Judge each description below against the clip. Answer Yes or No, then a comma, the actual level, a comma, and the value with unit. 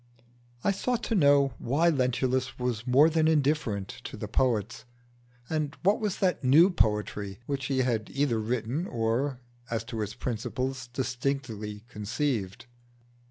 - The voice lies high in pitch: No, low, 130 Hz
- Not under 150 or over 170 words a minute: No, average, 140 wpm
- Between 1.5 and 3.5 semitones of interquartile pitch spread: No, average, 4.2 semitones